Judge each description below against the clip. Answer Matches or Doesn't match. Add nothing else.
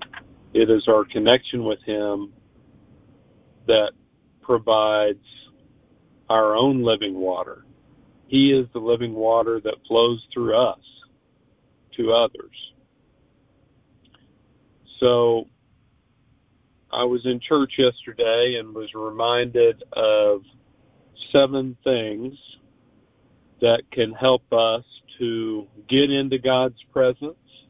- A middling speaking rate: Doesn't match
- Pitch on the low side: Matches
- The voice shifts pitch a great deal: Doesn't match